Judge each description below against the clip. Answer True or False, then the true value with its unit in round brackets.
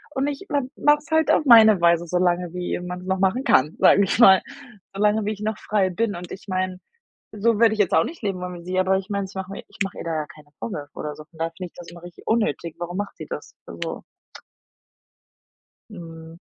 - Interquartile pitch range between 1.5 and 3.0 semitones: False (3.6 semitones)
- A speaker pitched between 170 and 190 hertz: True (185 Hz)